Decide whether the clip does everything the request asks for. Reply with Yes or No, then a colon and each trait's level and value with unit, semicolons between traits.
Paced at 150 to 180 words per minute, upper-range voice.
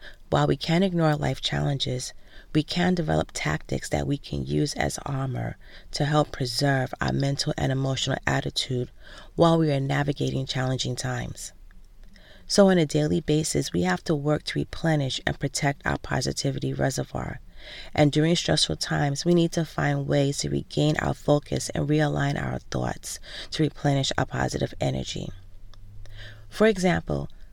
No: average, 155 wpm; low, 135 Hz